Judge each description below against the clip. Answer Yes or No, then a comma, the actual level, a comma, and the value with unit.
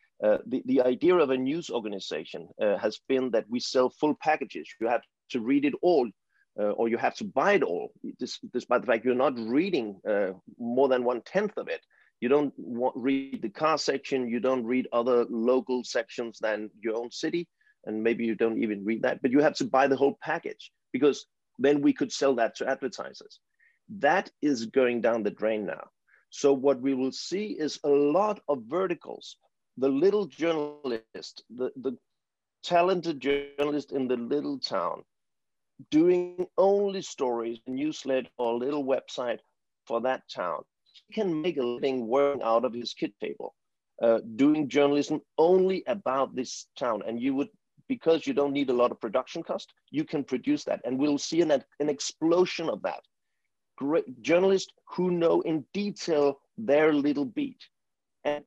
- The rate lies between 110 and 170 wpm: No, average, 180 wpm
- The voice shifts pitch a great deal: Yes, wide, 6.0 semitones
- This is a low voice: No, medium, 145 Hz